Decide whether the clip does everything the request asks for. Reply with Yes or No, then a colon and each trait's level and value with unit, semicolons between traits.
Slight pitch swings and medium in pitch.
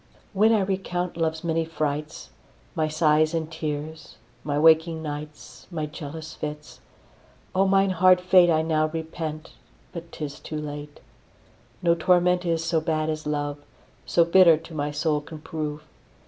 Yes: narrow, 1.9 semitones; medium, 160 Hz